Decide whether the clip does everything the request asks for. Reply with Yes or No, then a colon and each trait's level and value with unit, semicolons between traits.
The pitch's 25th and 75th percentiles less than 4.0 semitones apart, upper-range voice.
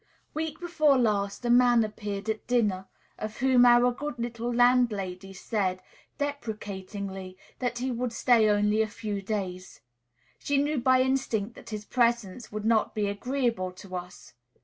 Yes: average, 3.5 semitones; high, 225 Hz